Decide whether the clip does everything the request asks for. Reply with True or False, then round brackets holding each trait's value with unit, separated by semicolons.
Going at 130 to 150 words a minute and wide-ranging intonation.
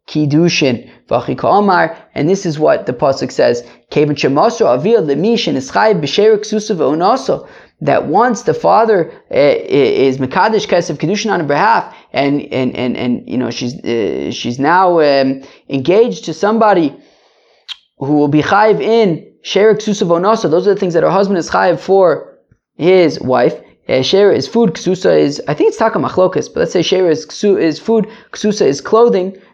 True (140 wpm; 6.2 semitones)